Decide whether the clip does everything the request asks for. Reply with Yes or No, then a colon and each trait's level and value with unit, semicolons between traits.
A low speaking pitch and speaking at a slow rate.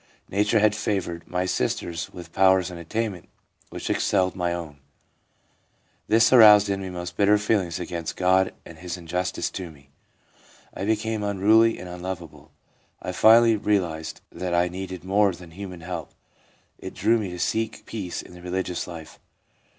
No: very low, 95 Hz; average, 165 wpm